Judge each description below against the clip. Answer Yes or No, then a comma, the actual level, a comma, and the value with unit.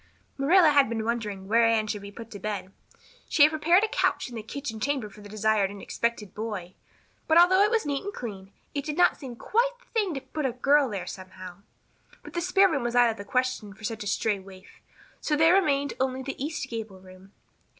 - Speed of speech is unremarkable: No, fast, 230 wpm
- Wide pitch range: Yes, wide, 6.4 semitones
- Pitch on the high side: Yes, high, 235 Hz